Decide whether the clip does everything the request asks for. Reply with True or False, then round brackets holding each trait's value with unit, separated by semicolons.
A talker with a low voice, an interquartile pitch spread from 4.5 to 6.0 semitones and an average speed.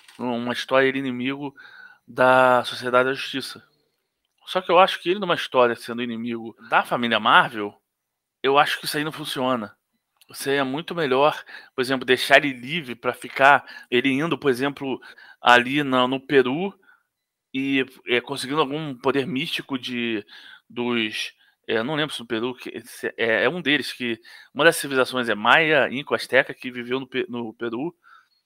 False (130 Hz; 2.4 semitones; 165 wpm)